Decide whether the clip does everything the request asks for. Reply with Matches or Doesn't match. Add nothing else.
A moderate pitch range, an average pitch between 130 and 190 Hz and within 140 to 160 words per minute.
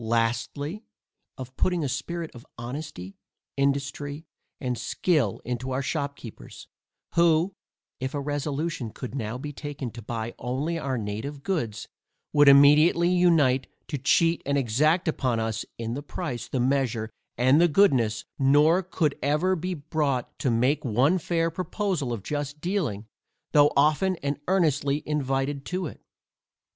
Matches